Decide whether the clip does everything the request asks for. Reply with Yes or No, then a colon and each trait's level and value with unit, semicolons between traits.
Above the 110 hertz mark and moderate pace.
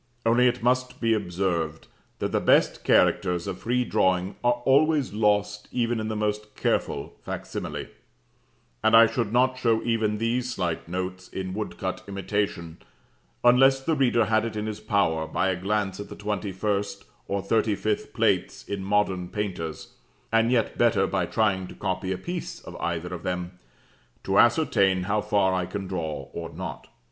No: low, 105 Hz; average, 165 wpm